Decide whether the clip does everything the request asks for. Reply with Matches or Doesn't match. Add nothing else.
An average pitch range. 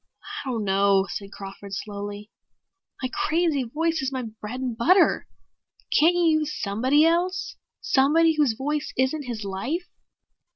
Doesn't match